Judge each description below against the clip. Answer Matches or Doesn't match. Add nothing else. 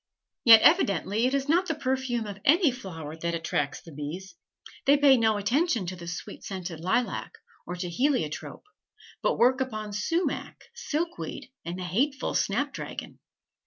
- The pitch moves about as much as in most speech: Doesn't match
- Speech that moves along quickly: Doesn't match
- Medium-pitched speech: Doesn't match